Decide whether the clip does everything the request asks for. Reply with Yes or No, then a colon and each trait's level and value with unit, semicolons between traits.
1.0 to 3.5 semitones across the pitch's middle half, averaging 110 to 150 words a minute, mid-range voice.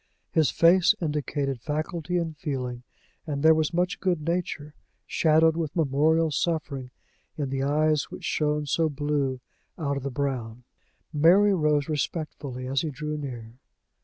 Yes: average, 2.7 semitones; average, 145 wpm; medium, 150 Hz